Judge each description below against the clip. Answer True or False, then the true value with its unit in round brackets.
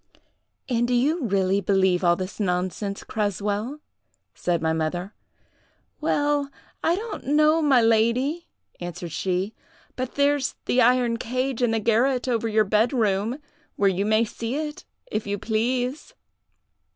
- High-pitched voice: True (230 Hz)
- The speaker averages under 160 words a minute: True (140 wpm)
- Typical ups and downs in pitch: True (4.7 semitones)